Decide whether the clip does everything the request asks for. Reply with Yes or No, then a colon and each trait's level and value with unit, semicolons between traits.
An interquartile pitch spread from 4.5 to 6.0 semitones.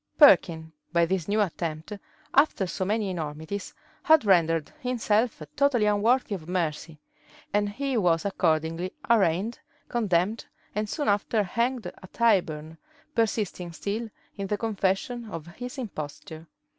Yes: average, 5.2 semitones